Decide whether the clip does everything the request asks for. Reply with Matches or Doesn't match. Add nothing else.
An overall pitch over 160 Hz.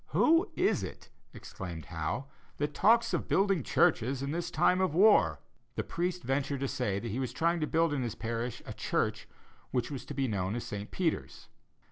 Doesn't match